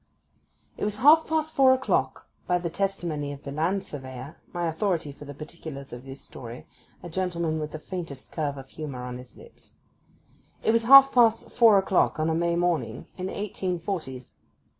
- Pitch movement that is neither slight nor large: No, wide, 5.7 semitones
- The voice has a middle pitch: Yes, medium, 170 Hz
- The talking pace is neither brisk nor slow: Yes, average, 185 wpm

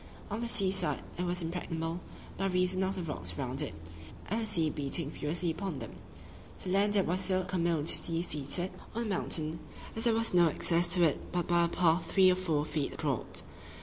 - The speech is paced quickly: Yes, fast, 210 wpm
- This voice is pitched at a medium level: Yes, medium, 175 Hz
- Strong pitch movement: No, average, 2.7 semitones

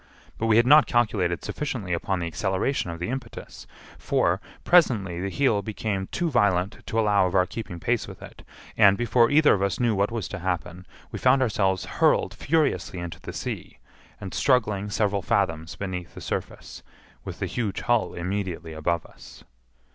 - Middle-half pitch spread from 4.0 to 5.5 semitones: Yes, average, 4.6 semitones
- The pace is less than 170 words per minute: No, average, 175 wpm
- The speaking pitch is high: No, low, 100 Hz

